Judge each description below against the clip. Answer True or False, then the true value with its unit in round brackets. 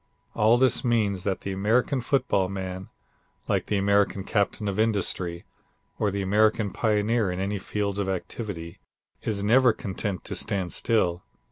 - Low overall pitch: True (100 Hz)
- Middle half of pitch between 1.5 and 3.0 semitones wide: True (2.4 semitones)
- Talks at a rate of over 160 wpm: False (150 wpm)